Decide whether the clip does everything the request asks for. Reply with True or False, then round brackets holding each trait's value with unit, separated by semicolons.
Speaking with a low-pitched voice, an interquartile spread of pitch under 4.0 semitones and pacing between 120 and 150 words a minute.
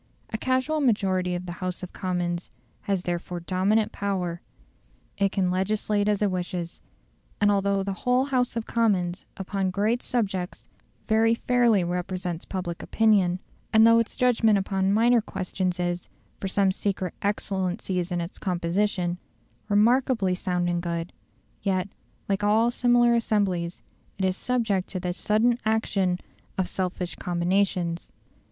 False (195 Hz; 3.3 semitones; 140 wpm)